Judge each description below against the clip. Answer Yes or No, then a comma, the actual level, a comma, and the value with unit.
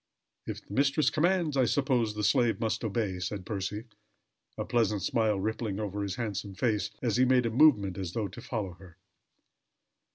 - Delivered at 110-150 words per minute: No, average, 175 wpm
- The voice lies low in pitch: Yes, low, 110 Hz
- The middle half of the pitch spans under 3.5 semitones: No, average, 3.9 semitones